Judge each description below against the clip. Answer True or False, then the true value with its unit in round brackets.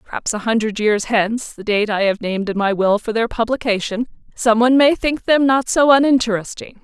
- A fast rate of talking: False (195 wpm)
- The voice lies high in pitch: True (230 Hz)